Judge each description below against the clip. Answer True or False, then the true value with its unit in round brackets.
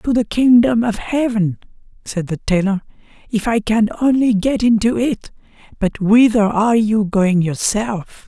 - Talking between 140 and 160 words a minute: True (145 wpm)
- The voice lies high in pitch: True (220 Hz)